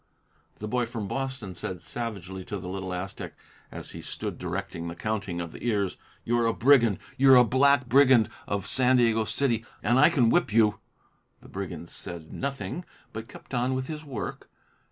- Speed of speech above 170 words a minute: Yes, average, 180 wpm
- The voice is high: No, low, 115 Hz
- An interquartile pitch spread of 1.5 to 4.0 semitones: No, average, 5.2 semitones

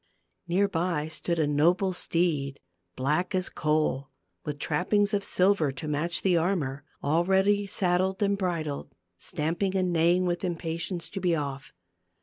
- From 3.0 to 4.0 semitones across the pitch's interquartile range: Yes, average, 3.6 semitones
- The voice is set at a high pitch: No, medium, 175 Hz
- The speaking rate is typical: Yes, average, 145 wpm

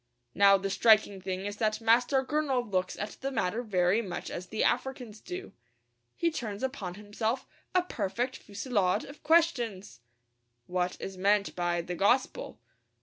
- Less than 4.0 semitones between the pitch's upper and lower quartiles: No, average, 4.8 semitones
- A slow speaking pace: No, average, 150 wpm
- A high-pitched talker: Yes, high, 210 Hz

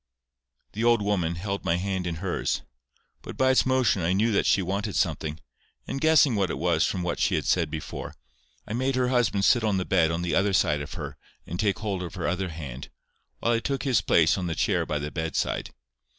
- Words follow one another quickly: Yes, fast, 225 wpm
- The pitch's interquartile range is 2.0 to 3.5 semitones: No, average, 4.7 semitones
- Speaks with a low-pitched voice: Yes, very low, 95 Hz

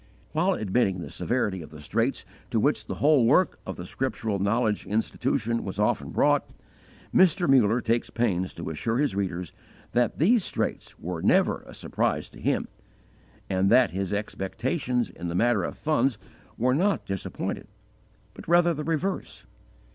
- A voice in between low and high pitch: No, low, 115 Hz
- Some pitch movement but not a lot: No, wide, 6.3 semitones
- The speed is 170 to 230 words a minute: No, average, 160 wpm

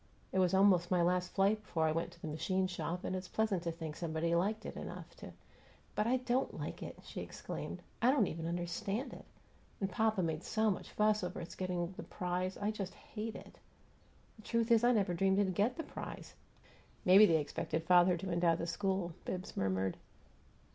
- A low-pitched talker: No, medium, 185 Hz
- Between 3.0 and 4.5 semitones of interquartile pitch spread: Yes, average, 3.7 semitones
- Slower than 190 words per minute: No, fast, 205 wpm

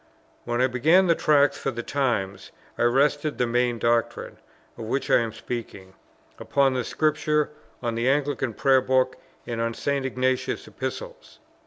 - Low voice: Yes, low, 130 Hz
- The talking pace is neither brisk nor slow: Yes, average, 155 wpm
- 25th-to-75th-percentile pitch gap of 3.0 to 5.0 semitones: Yes, average, 3.3 semitones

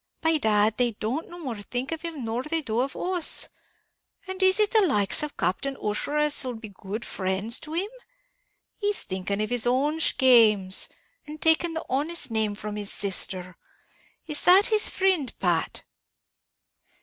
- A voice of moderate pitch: No, very high, 255 Hz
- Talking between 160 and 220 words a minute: Yes, average, 165 wpm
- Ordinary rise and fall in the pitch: No, wide, 7.4 semitones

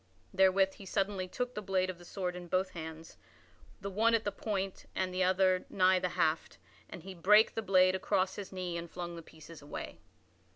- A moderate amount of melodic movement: No, narrow, 1.6 semitones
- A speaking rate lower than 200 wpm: No, fast, 205 wpm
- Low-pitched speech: No, medium, 185 Hz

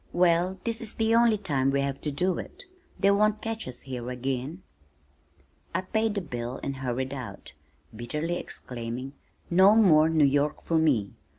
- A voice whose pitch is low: No, medium, 155 Hz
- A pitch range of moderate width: No, wide, 7.0 semitones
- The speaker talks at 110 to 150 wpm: No, average, 170 wpm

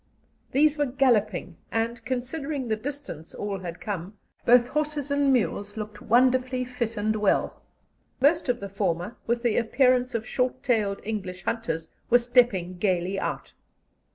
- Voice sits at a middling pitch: No, high, 235 Hz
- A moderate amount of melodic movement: Yes, average, 4.1 semitones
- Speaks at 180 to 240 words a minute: No, average, 150 wpm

